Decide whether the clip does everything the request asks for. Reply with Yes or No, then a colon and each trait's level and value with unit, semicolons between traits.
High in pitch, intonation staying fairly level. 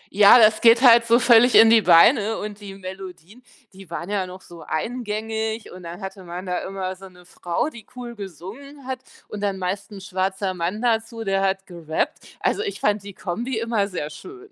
No: high, 200 Hz; average, 3.7 semitones